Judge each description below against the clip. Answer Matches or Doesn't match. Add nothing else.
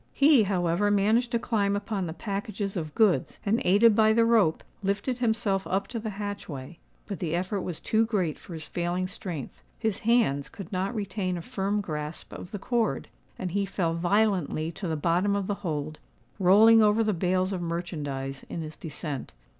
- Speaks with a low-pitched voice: Doesn't match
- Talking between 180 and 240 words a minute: Matches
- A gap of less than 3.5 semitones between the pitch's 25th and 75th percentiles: Doesn't match